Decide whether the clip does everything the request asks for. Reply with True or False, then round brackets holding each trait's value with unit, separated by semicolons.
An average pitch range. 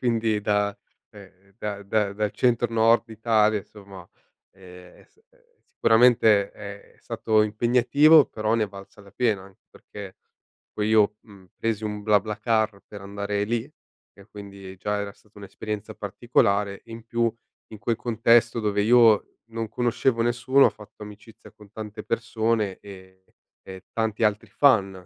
False (2.3 semitones)